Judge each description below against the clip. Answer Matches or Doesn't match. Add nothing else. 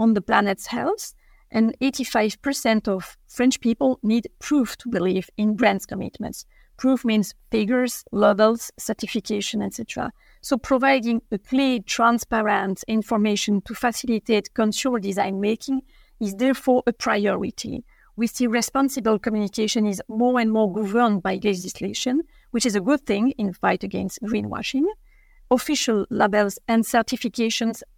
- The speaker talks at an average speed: Doesn't match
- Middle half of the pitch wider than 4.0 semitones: Doesn't match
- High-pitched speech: Matches